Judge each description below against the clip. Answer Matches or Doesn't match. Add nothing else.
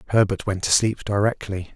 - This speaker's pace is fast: Doesn't match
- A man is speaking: Matches